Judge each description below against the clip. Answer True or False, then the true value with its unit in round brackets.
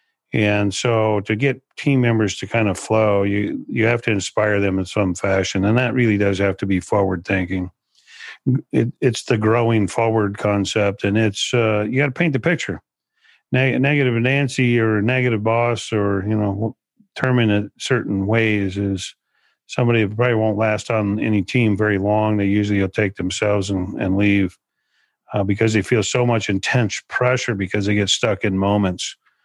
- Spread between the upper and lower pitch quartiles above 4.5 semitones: False (2.9 semitones)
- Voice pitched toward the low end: True (105 Hz)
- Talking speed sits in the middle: True (180 wpm)